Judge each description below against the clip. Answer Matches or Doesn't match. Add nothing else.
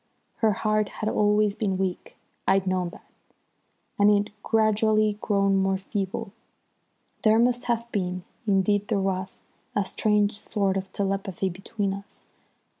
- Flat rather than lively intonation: Matches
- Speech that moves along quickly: Doesn't match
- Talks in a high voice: Matches